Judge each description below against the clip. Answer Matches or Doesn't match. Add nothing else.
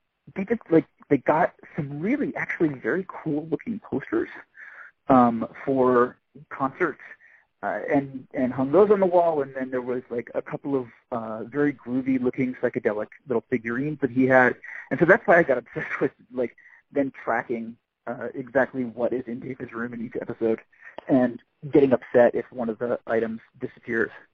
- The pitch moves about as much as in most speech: Matches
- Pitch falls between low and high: Doesn't match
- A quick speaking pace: Doesn't match